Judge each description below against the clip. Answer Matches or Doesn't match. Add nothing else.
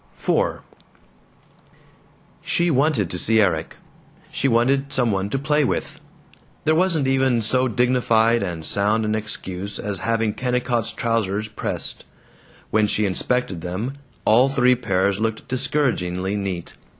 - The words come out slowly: Matches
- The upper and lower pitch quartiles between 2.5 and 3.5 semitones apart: Doesn't match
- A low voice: Matches